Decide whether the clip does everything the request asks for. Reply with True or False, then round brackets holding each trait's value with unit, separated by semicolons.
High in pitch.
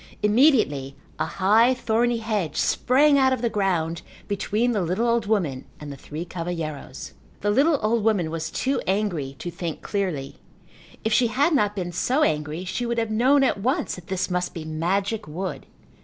True (200 Hz)